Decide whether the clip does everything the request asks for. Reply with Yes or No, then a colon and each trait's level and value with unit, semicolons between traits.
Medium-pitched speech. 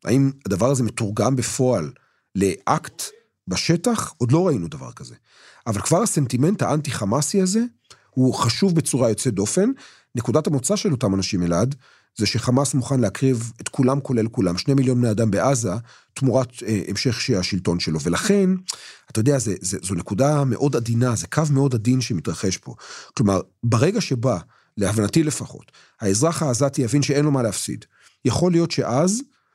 No: low, 130 Hz